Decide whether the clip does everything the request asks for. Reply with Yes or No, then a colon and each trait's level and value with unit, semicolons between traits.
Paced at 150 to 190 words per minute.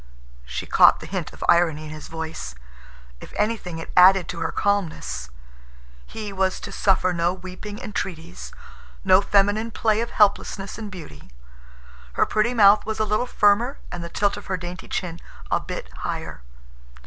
Yes: average, 165 wpm